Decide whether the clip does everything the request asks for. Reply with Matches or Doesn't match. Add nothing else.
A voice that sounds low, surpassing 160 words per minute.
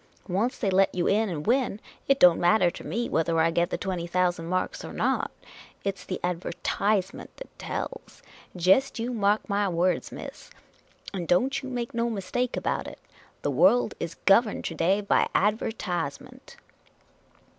Doesn't match